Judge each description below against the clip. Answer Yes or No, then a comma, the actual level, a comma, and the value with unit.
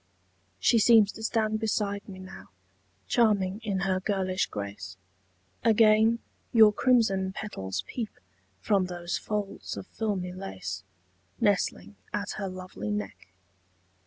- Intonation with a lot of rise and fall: No, average, 2.7 semitones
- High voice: Yes, high, 195 Hz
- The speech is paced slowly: Yes, slow, 120 wpm